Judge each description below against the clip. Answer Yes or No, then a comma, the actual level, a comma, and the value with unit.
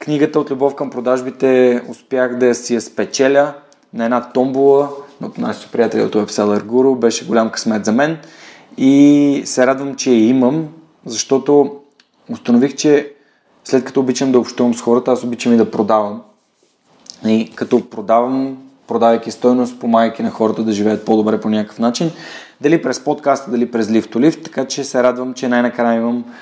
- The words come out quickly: Yes, fast, 170 wpm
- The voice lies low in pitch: Yes, low, 125 Hz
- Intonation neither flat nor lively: Yes, average, 3.3 semitones